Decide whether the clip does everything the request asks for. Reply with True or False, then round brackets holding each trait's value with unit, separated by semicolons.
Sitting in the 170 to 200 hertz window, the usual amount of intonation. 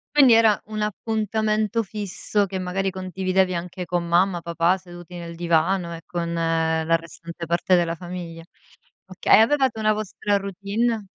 True (185 Hz; 3.7 semitones)